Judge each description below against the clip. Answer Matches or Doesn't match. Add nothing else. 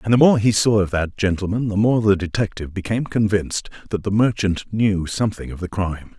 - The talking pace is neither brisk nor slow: Doesn't match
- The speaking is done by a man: Matches